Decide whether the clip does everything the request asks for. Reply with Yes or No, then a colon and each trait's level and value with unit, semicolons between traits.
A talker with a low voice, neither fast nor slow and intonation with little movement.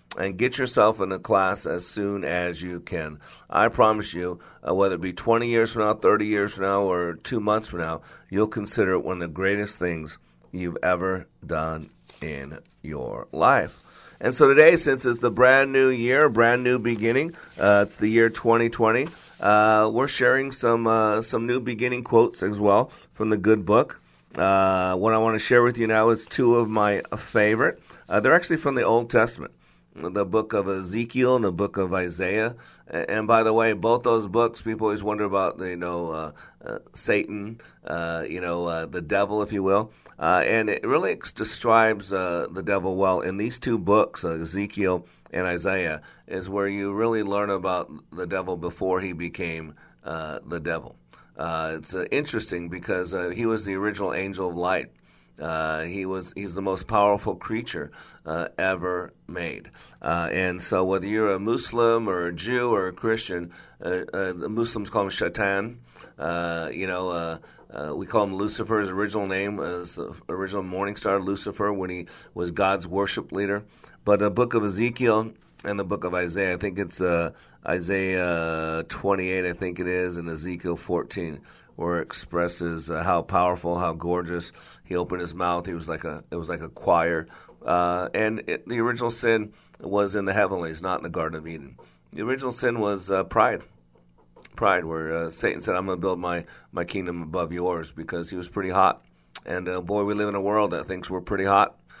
No: very low, 95 Hz; average, 195 wpm; average, 3.7 semitones